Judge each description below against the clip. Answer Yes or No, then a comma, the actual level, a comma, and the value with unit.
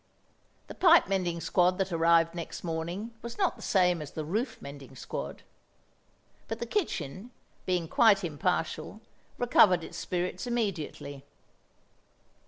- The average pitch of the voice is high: No, medium, 180 Hz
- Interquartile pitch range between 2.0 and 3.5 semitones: No, average, 4.7 semitones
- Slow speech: Yes, slow, 130 wpm